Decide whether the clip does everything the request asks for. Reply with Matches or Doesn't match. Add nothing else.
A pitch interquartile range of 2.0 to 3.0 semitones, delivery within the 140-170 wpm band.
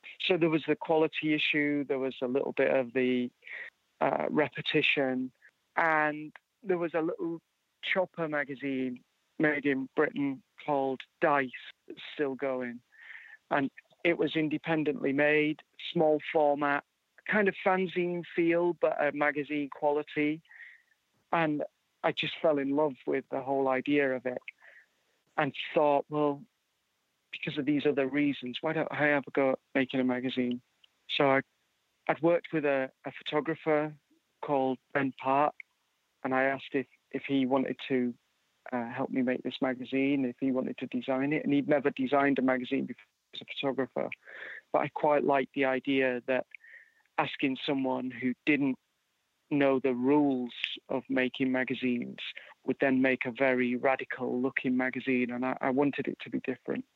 Matches